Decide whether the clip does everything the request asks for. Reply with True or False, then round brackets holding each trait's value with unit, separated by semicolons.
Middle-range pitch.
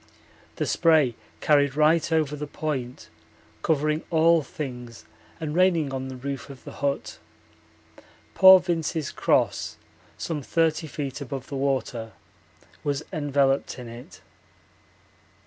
True (145 Hz)